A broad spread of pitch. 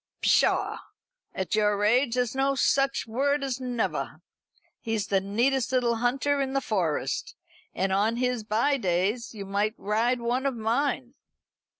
No: average, 3.9 semitones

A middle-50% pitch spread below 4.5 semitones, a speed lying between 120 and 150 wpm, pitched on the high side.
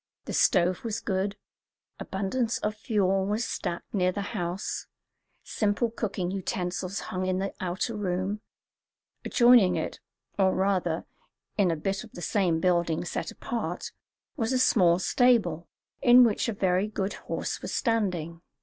Yes: average, 3.1 semitones; average, 145 wpm; high, 195 Hz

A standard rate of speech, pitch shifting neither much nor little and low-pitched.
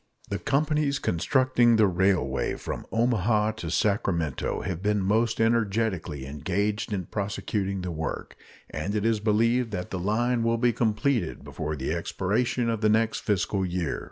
Yes: average, 155 wpm; average, 4.1 semitones; low, 105 Hz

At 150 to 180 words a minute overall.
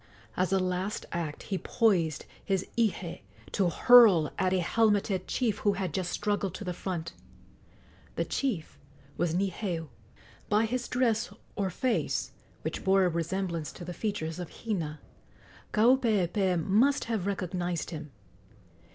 No: average, 140 wpm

